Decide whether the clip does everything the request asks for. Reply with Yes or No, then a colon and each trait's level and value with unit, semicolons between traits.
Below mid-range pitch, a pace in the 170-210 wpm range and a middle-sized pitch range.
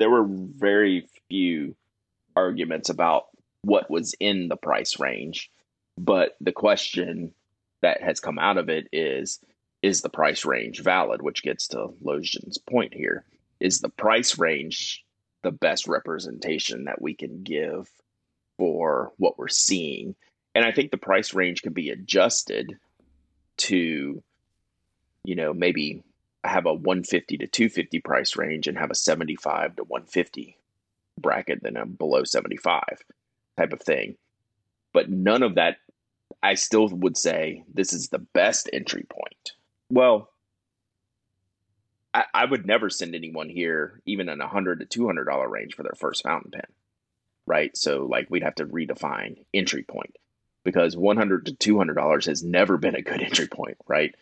No: low, 100 Hz; average, 160 wpm; average, 3.6 semitones